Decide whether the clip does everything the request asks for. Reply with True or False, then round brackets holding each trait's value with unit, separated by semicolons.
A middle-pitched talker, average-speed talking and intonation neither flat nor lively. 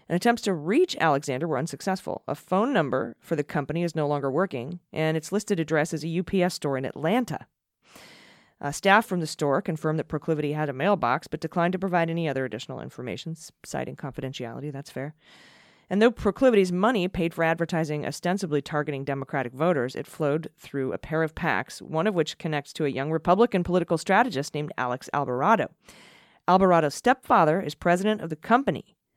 True (160 Hz; 180 wpm; 3.8 semitones)